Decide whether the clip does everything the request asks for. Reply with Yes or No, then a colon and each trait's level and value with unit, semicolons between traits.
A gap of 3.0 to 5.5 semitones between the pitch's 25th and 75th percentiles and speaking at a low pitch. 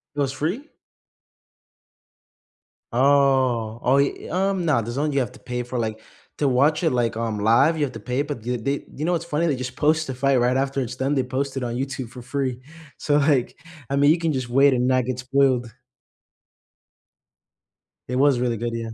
No: narrow, 2.6 semitones; low, 130 Hz